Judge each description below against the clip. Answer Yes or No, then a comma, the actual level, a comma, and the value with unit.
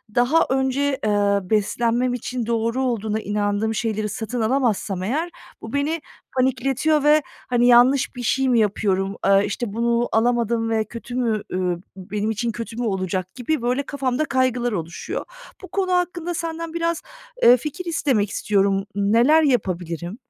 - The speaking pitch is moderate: No, high, 235 Hz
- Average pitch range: Yes, average, 4.3 semitones